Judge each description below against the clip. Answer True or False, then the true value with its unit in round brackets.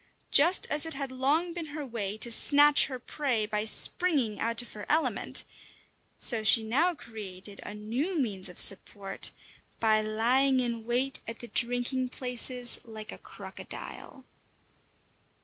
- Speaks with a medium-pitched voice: False (240 Hz)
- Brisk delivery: False (150 wpm)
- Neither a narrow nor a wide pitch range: True (4.2 semitones)